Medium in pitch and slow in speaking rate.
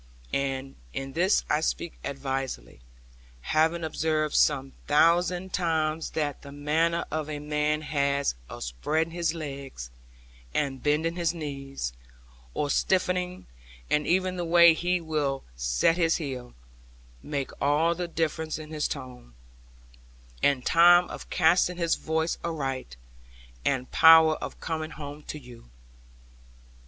Yes: medium, 155 Hz; slow, 125 wpm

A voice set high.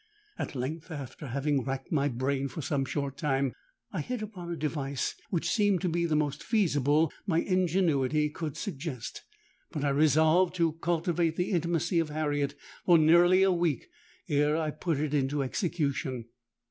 No: medium, 155 Hz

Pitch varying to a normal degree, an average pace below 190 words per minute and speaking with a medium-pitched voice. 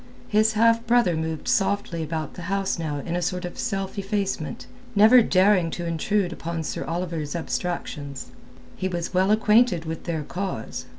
Yes: average, 3.7 semitones; average, 165 wpm; medium, 180 Hz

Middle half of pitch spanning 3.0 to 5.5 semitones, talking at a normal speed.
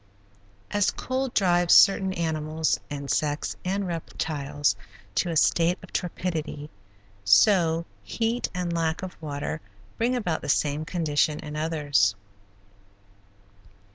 No: average, 3.4 semitones; slow, 110 wpm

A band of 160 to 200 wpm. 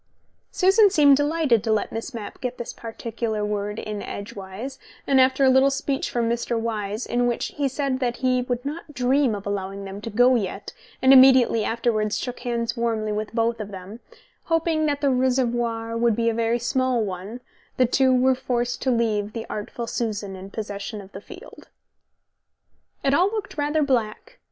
Yes: average, 180 wpm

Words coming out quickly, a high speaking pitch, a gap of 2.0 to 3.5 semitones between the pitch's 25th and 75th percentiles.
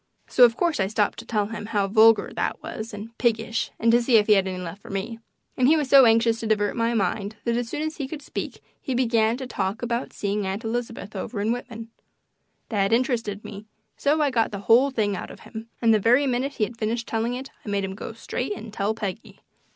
Yes: fast, 245 wpm; high, 225 Hz; average, 2.7 semitones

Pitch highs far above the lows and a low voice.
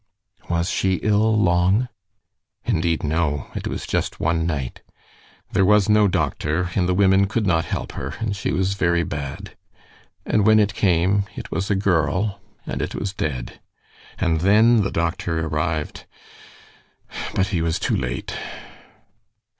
No: average, 3.5 semitones; very low, 90 Hz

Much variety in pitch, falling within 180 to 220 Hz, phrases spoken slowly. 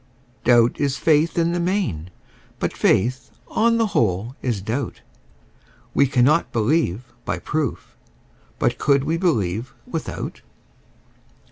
No: wide, 6.3 semitones; low, 135 Hz; slow, 120 wpm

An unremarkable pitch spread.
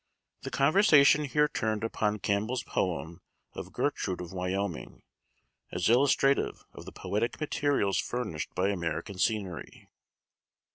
No: wide, 6.9 semitones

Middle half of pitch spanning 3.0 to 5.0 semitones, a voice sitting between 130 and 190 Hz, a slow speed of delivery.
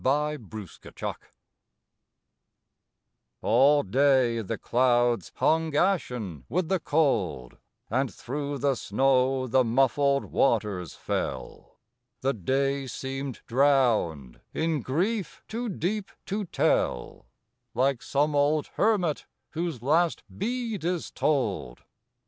Yes: average, 4.7 semitones; low, 135 Hz; slow, 100 wpm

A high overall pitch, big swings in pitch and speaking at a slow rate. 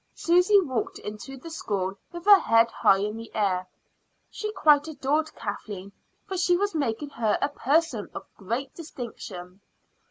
No: very high, 265 Hz; wide, 7.6 semitones; average, 155 wpm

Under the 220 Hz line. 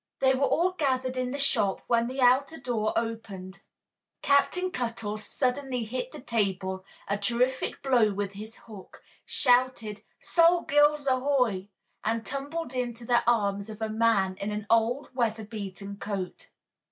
No: high, 235 Hz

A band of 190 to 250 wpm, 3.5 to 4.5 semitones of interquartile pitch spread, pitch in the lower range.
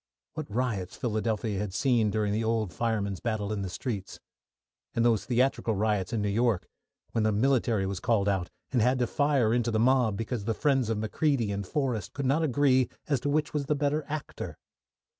Yes: average, 195 wpm; average, 4.0 semitones; low, 115 Hz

